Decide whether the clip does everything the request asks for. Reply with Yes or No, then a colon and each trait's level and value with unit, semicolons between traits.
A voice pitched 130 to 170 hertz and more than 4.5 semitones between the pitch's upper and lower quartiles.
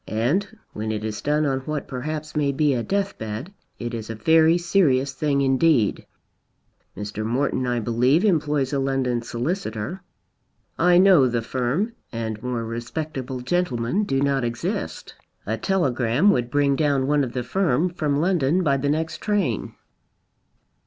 Yes: low, 135 Hz; average, 4.9 semitones